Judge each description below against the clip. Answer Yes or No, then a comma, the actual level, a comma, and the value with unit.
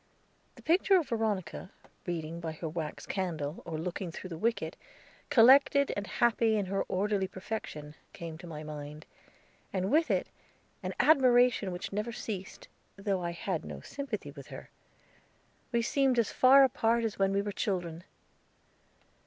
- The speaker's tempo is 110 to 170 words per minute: Yes, average, 155 wpm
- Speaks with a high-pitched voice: Yes, high, 195 Hz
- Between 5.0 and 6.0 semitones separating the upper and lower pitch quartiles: Yes, wide, 5.5 semitones